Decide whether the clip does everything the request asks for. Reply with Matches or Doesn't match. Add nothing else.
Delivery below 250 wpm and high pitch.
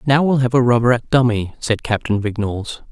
Doesn't match